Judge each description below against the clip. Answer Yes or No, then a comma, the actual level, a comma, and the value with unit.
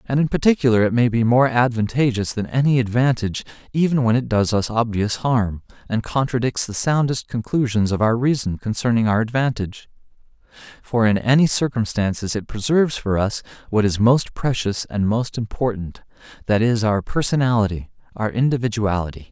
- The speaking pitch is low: Yes, low, 115 Hz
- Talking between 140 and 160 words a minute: Yes, average, 150 wpm